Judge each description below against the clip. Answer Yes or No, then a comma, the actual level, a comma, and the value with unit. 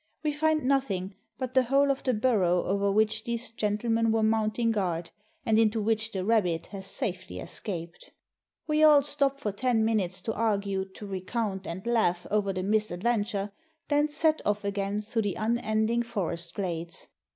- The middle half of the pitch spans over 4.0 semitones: No, average, 3.5 semitones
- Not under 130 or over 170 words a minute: Yes, average, 165 wpm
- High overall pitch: Yes, high, 215 Hz